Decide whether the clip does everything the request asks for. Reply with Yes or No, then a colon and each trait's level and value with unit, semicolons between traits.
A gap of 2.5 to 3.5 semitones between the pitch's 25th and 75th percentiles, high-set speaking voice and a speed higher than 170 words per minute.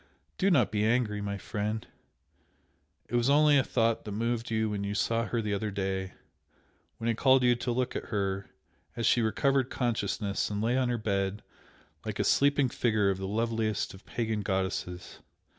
No: average, 3.1 semitones; low, 110 Hz; average, 185 wpm